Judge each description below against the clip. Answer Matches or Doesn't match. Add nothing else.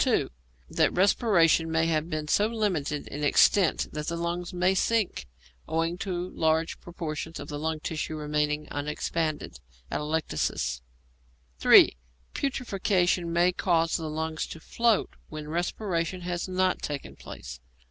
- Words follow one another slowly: Matches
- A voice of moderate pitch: Matches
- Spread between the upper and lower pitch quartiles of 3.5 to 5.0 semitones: Doesn't match